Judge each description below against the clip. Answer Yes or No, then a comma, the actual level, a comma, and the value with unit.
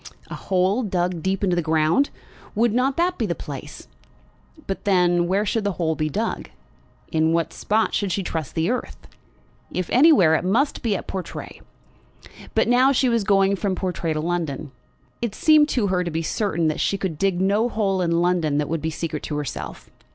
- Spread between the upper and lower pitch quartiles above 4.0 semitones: Yes, average, 4.4 semitones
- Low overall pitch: No, medium, 185 Hz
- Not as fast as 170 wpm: No, average, 195 wpm